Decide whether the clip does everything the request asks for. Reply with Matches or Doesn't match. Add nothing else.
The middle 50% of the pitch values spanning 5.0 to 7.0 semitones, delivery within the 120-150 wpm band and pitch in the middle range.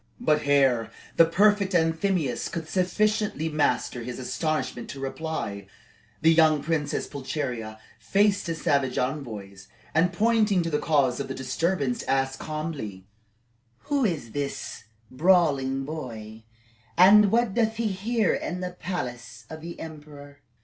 Matches